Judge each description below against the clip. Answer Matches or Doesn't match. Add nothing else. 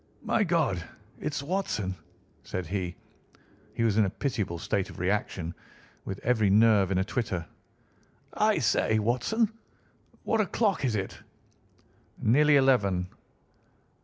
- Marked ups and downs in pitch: Matches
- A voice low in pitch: Matches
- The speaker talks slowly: Matches